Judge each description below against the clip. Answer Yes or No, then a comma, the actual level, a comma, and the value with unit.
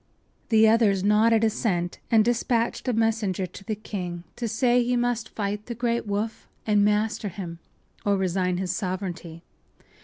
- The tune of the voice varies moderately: Yes, average, 3.2 semitones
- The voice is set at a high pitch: Yes, high, 210 Hz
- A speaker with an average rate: Yes, average, 160 wpm